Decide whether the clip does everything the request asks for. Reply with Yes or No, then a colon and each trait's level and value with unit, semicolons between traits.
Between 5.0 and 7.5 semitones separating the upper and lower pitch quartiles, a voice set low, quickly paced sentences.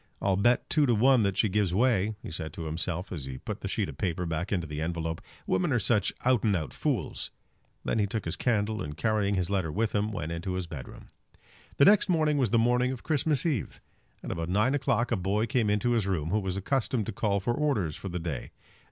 Yes: wide, 5.5 semitones; low, 100 Hz; fast, 240 wpm